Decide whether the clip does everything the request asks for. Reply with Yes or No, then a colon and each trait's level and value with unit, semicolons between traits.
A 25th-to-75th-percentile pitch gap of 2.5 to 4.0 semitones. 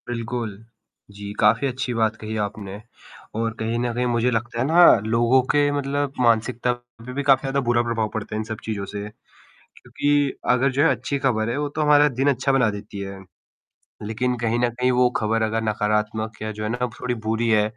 Yes: average, 3.0 semitones